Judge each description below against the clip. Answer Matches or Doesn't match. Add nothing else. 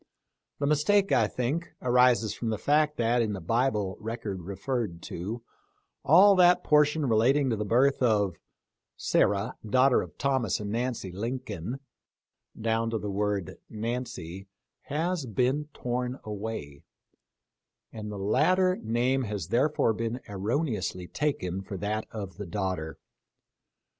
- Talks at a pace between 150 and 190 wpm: Doesn't match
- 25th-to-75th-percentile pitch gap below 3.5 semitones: Doesn't match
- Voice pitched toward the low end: Matches